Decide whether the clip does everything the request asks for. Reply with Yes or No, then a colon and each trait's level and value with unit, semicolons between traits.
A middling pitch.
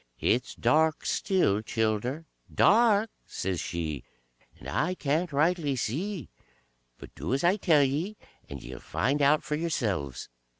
Yes: medium, 145 Hz